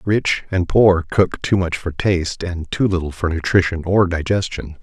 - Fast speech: No, average, 185 wpm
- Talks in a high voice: No, very low, 90 Hz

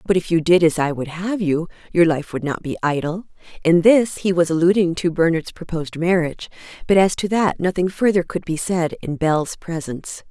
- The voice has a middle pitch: Yes, medium, 170 Hz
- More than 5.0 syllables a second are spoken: Yes, 5.3 syllables/s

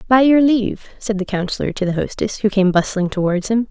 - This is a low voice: No, high, 210 Hz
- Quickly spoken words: Yes, fast, 225 wpm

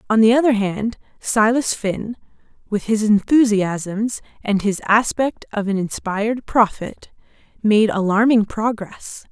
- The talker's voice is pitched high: Yes, high, 215 Hz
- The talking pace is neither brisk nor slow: No, slow, 120 wpm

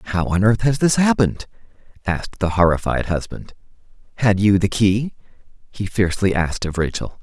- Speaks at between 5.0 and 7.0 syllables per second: Yes, 5.4 syllables/s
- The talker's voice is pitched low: Yes, low, 100 Hz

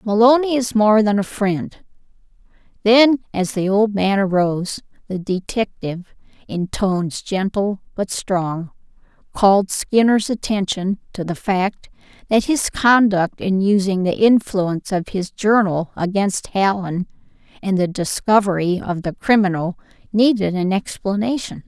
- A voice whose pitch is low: No, high, 200 Hz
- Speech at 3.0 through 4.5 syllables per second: Yes, 4.1 syllables/s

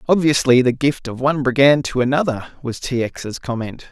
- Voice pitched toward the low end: Yes, low, 130 Hz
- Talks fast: No, average, 185 wpm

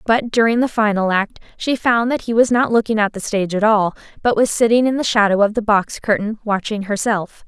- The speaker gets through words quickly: Yes, fast, 235 wpm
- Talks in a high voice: Yes, high, 220 Hz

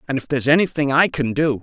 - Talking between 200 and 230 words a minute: No, fast, 260 wpm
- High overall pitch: No, medium, 140 Hz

